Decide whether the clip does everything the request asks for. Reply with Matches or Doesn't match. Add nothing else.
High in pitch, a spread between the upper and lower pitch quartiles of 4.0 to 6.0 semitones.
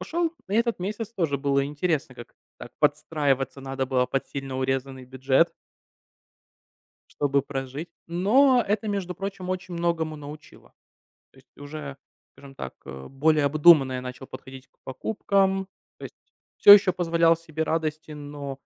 Doesn't match